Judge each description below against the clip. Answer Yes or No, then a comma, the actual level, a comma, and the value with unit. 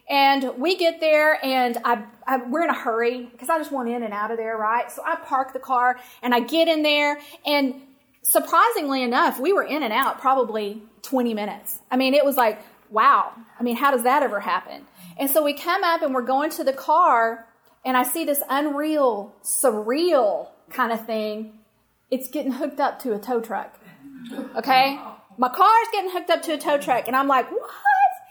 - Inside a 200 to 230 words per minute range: Yes, fast, 205 wpm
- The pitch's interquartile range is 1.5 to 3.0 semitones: No, average, 4.4 semitones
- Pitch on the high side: Yes, very high, 265 Hz